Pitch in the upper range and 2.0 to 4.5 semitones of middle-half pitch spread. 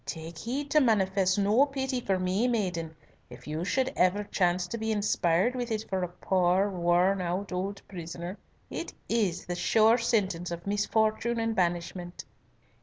Yes: high, 195 Hz; average, 4.0 semitones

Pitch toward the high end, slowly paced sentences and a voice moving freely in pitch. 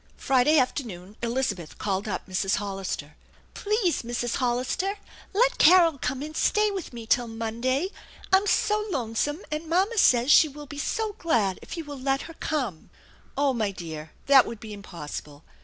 No: very high, 255 Hz; average, 175 wpm; wide, 7.2 semitones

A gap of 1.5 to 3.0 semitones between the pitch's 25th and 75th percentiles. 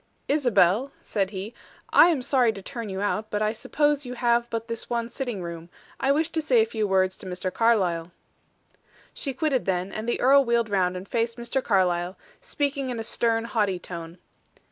No: average, 4.9 semitones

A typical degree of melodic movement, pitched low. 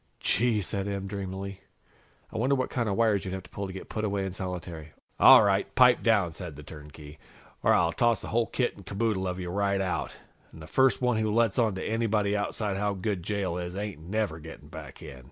Yes: average, 3.3 semitones; low, 100 Hz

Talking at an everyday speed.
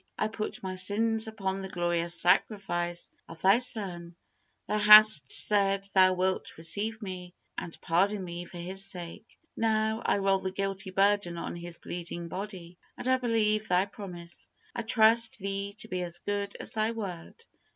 Yes: average, 165 wpm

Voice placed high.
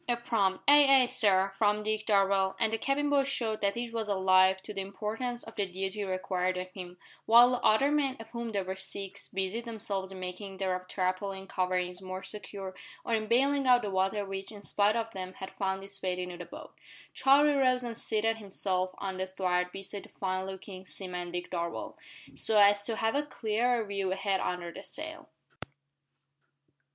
Yes: high, 200 Hz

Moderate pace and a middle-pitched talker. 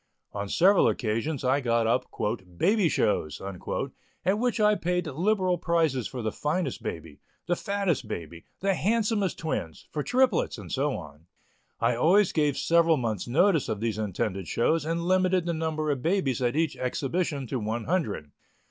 Yes: average, 165 wpm; medium, 155 Hz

